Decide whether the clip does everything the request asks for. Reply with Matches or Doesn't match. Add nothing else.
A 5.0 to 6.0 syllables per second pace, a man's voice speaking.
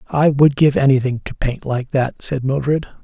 Doesn't match